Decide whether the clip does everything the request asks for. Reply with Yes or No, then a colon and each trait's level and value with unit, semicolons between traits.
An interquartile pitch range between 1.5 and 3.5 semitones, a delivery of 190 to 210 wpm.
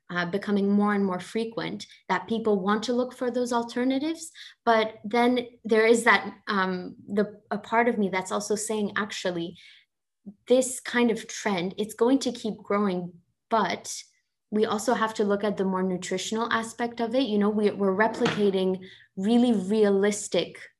No: average, 2.9 semitones; average, 165 wpm